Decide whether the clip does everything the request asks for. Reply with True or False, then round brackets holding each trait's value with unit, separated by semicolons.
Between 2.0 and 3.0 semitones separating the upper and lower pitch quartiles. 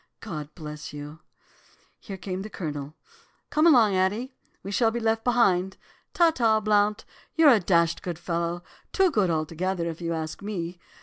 False (4.8 semitones)